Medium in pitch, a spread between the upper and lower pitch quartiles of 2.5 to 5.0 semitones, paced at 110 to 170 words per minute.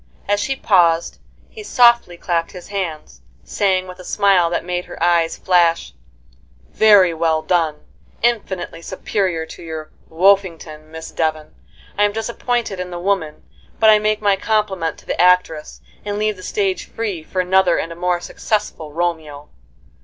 Yes: medium, 180 Hz; average, 3.6 semitones; average, 160 wpm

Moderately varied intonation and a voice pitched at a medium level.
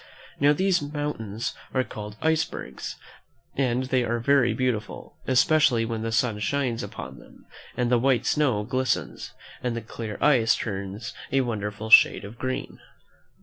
No: average, 3.5 semitones; low, 120 Hz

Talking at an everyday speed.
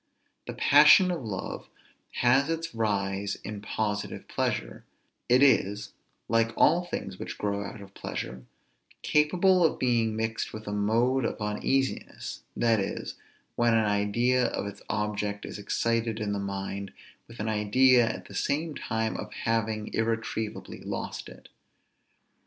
Yes: average, 145 wpm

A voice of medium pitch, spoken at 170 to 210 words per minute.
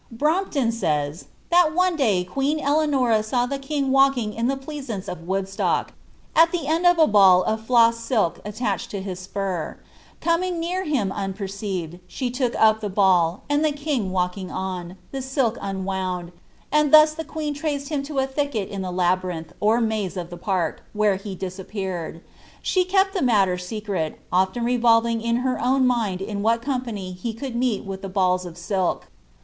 No: high, 220 Hz; average, 180 wpm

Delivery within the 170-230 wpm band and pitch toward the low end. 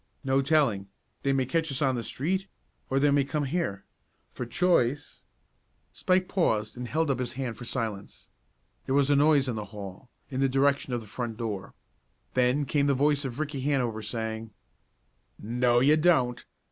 Yes: average, 185 wpm; low, 130 Hz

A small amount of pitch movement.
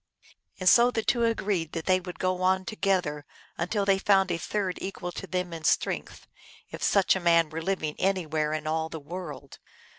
No: average, 3.2 semitones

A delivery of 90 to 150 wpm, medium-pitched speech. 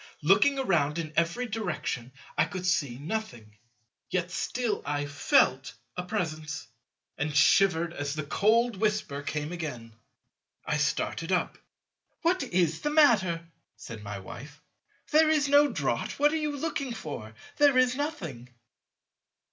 Yes: average, 140 wpm; medium, 170 Hz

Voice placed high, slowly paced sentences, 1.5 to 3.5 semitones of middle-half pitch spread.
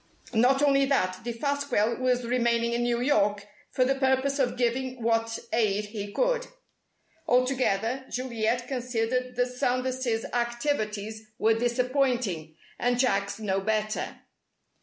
Yes: high, 240 Hz; slow, 120 wpm; narrow, 2.6 semitones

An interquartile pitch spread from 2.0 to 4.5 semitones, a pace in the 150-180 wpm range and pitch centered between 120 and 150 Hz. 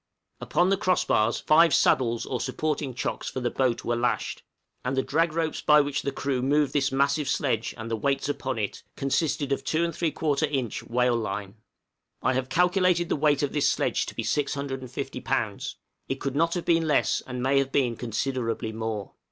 No: average, 3.4 semitones; average, 195 wpm; low, 135 Hz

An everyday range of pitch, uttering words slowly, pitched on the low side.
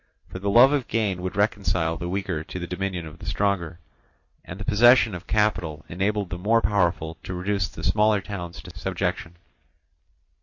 No: average, 3.2 semitones; average, 180 wpm; very low, 95 Hz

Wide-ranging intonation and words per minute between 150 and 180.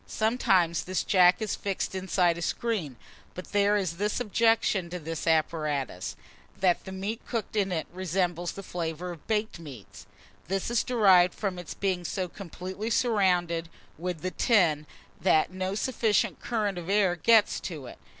No: average, 3.4 semitones; average, 160 wpm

